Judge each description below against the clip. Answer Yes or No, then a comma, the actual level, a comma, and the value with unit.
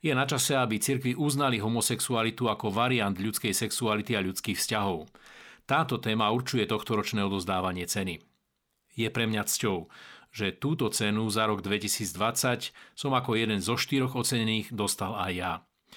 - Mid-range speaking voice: No, low, 110 Hz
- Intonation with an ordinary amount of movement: Yes, average, 3.0 semitones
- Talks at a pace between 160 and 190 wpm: No, average, 145 wpm